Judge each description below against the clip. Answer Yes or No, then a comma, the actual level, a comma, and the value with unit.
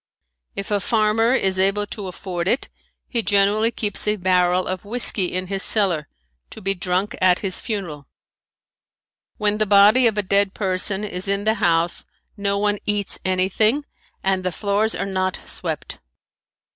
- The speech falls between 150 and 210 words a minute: Yes, average, 160 wpm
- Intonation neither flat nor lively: No, narrow, 2.3 semitones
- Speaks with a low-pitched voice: No, high, 200 Hz